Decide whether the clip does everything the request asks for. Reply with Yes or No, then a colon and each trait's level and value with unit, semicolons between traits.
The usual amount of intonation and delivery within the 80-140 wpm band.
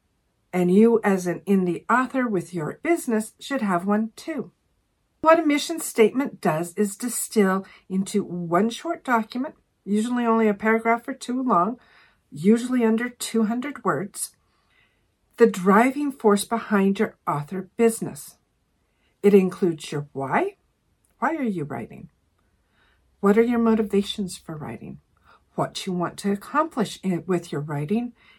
Yes: average, 4.7 semitones; slow, 135 wpm